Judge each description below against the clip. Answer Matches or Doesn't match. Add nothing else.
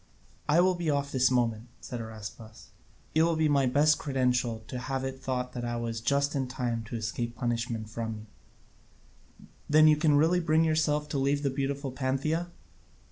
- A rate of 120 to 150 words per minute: Doesn't match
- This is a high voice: Doesn't match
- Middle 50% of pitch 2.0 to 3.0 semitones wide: Doesn't match